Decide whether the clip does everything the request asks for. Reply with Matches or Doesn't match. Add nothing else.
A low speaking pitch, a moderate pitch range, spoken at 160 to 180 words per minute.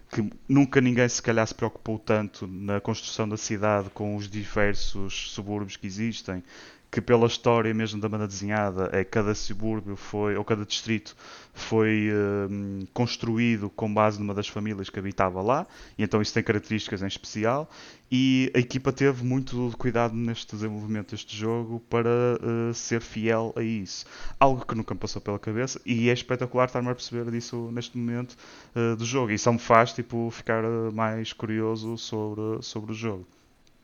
Doesn't match